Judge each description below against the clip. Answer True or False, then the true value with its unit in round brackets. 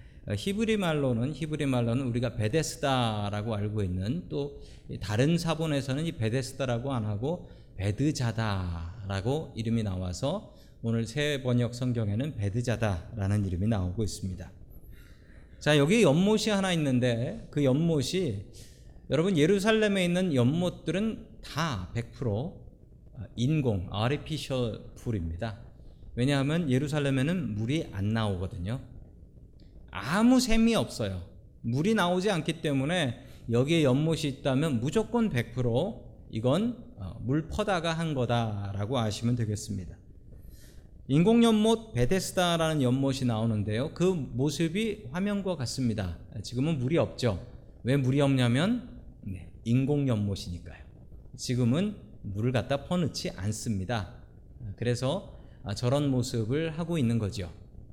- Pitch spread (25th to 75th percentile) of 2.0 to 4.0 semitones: False (6.2 semitones)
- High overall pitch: False (125 Hz)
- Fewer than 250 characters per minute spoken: False (275 characters per minute)